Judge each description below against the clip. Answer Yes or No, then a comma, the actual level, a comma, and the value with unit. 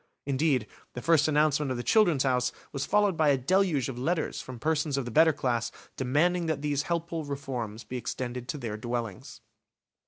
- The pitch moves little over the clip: No, average, 4.3 semitones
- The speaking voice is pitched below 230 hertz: Yes, medium, 140 Hz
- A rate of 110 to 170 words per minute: No, average, 185 wpm